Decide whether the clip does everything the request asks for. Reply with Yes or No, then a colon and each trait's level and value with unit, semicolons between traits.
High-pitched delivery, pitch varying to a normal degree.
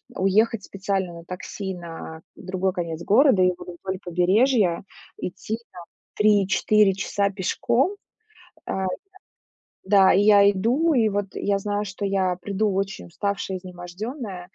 No: high, 195 Hz; narrow, 2.3 semitones